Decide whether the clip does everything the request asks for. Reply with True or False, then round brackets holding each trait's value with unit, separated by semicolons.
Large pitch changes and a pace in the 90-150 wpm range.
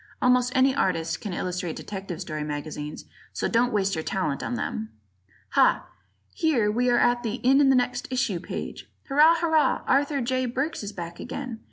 False (6.0 semitones; 175 wpm)